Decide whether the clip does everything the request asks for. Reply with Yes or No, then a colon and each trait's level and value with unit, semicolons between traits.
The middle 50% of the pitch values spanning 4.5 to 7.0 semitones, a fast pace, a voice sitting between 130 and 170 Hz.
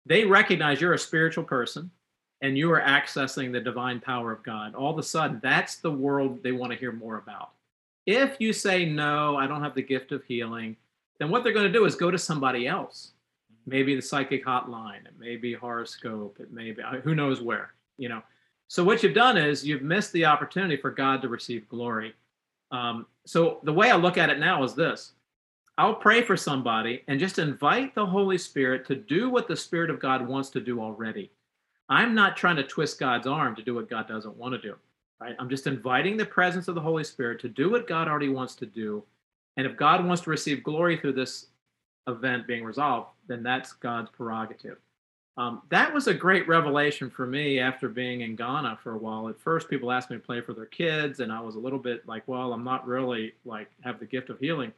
Yes: average, 5.2 semitones; fast, 220 wpm; low, 135 Hz